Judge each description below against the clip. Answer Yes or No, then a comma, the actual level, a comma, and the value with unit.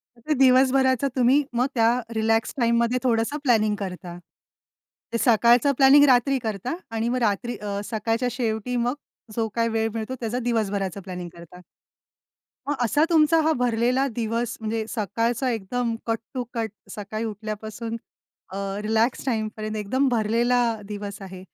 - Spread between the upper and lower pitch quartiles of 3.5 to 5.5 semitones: No, narrow, 2.6 semitones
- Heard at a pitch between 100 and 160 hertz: No, high, 230 Hz